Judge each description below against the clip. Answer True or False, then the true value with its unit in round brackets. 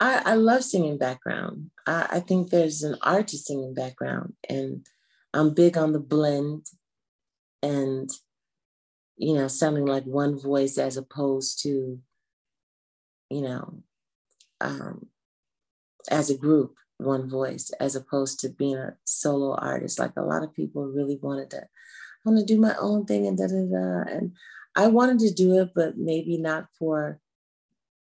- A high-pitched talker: False (140 Hz)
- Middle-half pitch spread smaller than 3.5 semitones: False (3.8 semitones)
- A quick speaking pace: False (155 wpm)